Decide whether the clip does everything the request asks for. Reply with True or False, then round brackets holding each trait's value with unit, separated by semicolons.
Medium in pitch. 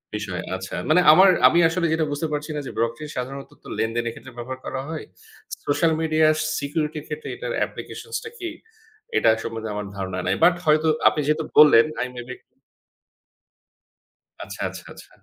True (145 Hz)